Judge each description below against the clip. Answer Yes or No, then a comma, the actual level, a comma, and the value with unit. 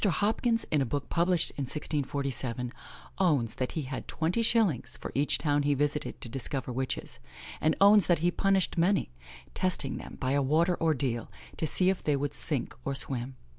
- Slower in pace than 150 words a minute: No, average, 180 wpm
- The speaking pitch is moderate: Yes, medium, 145 Hz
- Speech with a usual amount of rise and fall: Yes, average, 4.7 semitones